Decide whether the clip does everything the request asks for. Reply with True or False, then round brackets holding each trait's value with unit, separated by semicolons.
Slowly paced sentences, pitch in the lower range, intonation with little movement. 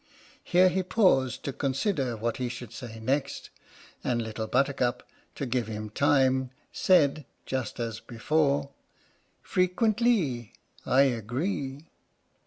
False (115 wpm; 130 Hz; 4.2 semitones)